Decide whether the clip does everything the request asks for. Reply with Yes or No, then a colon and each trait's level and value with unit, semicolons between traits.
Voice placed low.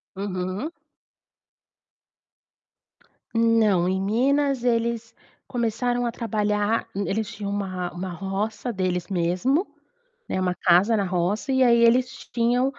No: high, 215 Hz